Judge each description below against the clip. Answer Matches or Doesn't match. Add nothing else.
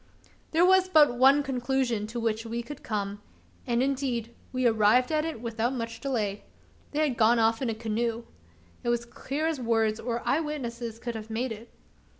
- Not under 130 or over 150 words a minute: Doesn't match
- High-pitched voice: Matches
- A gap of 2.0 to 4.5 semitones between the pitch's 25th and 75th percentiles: Matches